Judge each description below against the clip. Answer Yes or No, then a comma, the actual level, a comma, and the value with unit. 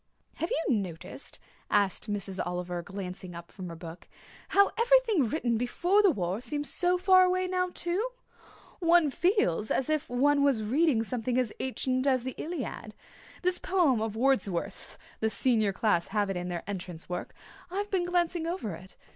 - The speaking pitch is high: Yes, very high, 255 Hz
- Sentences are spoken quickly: No, average, 170 wpm